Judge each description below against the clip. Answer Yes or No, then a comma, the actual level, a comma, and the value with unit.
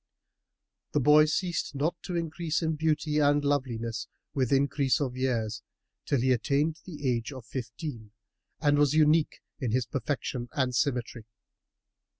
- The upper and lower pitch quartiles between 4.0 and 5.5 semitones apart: No, average, 3.6 semitones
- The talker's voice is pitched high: No, medium, 140 Hz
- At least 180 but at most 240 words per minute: No, average, 145 wpm